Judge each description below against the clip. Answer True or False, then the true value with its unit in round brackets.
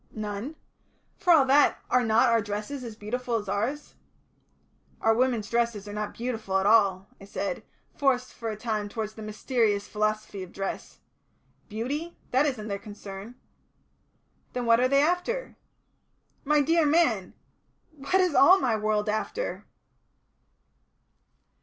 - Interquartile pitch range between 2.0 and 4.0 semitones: False (4.6 semitones)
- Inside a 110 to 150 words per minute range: True (140 wpm)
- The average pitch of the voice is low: False (230 Hz)